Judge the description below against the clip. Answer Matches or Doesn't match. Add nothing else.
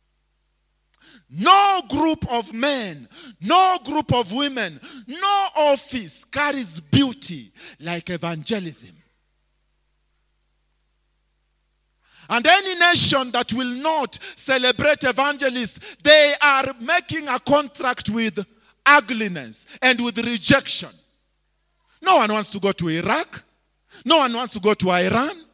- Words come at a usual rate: Doesn't match